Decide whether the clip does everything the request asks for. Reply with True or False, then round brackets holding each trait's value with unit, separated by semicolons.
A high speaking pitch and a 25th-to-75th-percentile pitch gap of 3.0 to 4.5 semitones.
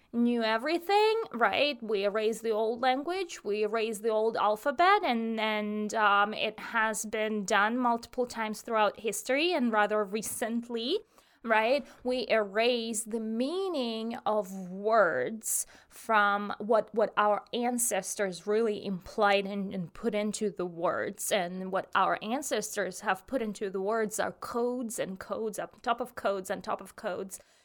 False (220 Hz; 2.6 semitones)